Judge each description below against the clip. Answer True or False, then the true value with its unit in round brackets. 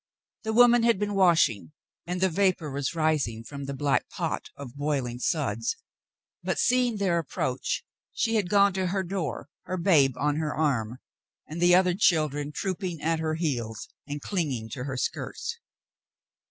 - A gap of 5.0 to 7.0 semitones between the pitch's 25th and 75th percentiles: True (5.3 semitones)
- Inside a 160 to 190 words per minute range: True (165 wpm)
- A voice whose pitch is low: False (160 Hz)